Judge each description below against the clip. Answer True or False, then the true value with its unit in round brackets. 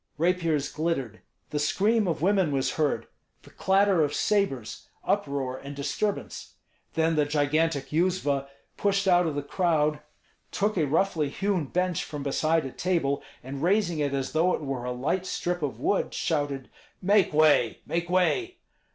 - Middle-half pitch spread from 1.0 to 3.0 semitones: False (4.4 semitones)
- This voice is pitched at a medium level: True (160 Hz)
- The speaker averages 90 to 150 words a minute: False (160 wpm)